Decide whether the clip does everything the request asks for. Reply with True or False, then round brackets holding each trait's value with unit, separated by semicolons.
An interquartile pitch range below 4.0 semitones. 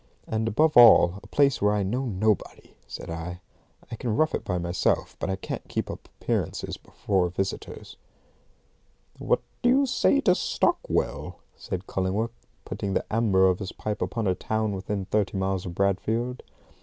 True (3.5 semitones)